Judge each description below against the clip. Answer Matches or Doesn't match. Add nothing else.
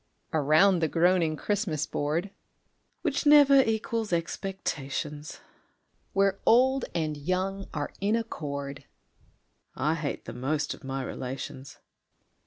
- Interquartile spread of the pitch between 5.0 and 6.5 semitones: Matches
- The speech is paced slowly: Matches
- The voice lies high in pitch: Doesn't match